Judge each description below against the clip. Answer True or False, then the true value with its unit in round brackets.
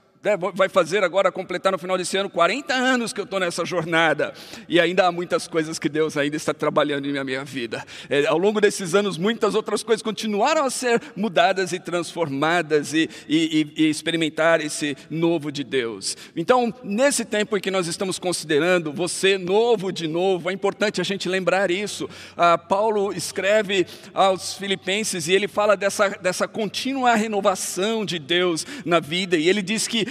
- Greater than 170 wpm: True (180 wpm)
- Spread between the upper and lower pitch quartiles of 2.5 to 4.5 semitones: True (3.5 semitones)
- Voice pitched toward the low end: False (190 Hz)